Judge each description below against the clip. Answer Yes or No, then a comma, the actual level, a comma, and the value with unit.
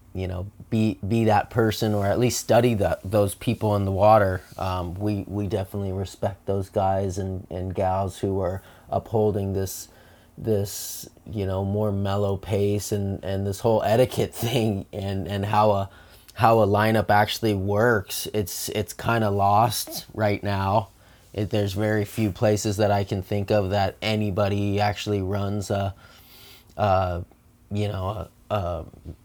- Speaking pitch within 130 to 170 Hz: No, low, 100 Hz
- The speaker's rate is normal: Yes, average, 160 wpm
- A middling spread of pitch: No, narrow, 1.8 semitones